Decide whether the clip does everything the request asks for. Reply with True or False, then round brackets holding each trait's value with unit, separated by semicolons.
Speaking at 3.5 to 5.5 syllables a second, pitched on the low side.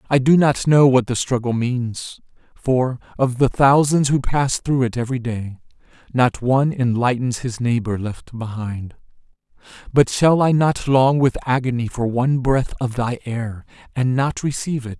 True (4.6 syllables/s; 125 Hz)